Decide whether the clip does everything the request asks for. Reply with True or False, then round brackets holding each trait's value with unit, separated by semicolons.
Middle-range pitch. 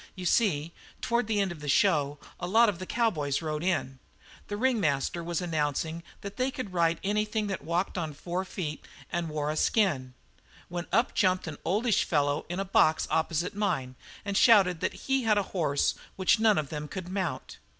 True (175 Hz)